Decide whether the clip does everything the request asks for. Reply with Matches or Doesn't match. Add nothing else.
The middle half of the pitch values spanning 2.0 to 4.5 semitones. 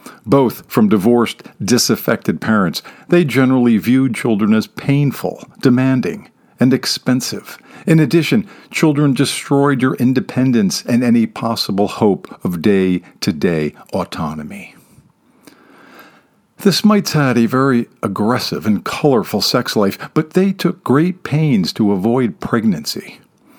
Doesn't match